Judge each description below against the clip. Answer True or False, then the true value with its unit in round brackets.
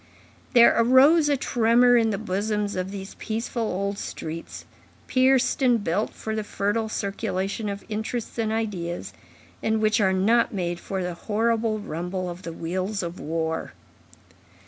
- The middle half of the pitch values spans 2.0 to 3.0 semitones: False (3.5 semitones)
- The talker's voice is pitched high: True (210 Hz)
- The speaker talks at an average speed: True (150 wpm)